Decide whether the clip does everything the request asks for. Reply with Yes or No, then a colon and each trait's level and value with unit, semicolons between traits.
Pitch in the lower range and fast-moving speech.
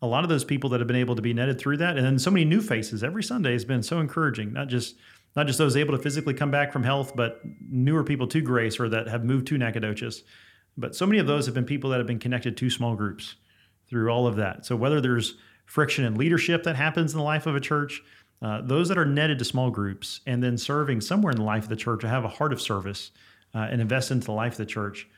Yes: low, 125 Hz; fast, 275 wpm